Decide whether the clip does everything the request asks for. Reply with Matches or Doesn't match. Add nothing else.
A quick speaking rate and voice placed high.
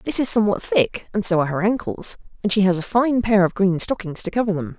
Matches